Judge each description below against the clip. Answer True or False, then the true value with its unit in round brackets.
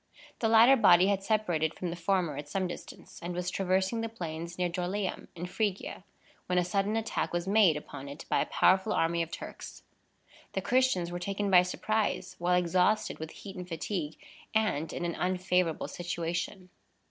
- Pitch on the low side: False (180 Hz)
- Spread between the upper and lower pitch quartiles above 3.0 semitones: False (2.7 semitones)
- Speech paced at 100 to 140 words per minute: False (180 wpm)